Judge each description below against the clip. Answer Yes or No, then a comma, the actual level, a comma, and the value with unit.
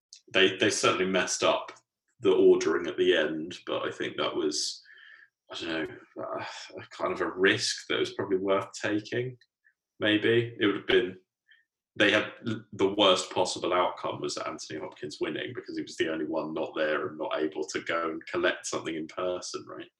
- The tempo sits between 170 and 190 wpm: Yes, average, 185 wpm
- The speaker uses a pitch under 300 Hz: No, very high, 365 Hz